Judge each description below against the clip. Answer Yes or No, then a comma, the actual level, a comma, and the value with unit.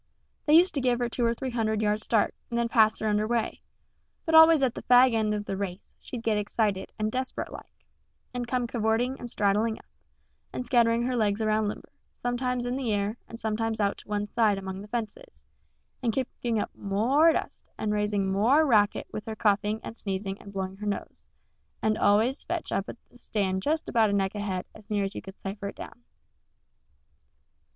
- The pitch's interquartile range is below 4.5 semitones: Yes, average, 2.9 semitones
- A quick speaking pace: Yes, fast, 220 wpm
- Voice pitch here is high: Yes, high, 220 Hz